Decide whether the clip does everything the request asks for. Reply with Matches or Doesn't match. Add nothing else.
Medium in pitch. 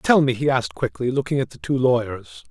Doesn't match